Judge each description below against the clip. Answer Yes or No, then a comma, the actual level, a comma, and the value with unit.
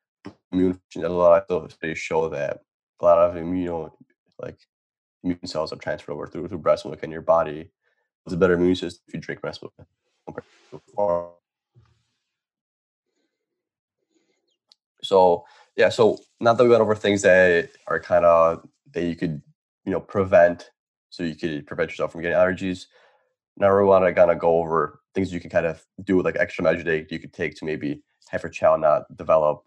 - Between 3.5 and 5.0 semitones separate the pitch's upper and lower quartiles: No, average, 2.8 semitones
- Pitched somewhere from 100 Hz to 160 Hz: No, very low, 90 Hz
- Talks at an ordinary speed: Yes, average, 180 wpm